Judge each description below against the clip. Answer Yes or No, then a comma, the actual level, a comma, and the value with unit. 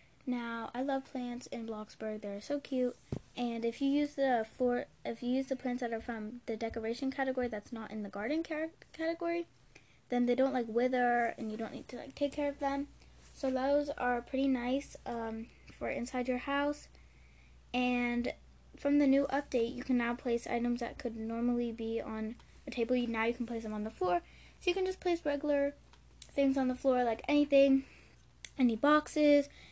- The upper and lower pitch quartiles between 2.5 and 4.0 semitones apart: Yes, average, 3.3 semitones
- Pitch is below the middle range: No, very high, 250 Hz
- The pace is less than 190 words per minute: No, average, 200 wpm